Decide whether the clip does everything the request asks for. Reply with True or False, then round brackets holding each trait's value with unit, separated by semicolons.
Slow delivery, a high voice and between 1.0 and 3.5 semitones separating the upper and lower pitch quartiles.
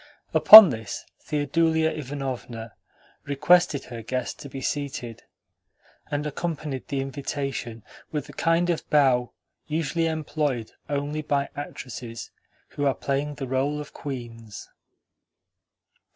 False (115 wpm; 140 Hz; 2.9 semitones)